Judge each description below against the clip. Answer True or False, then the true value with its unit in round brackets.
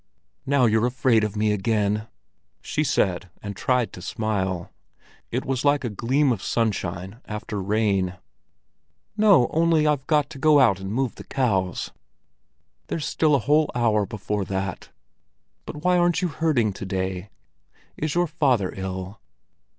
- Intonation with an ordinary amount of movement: False (6.5 semitones)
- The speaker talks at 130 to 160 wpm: True (150 wpm)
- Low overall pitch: True (115 Hz)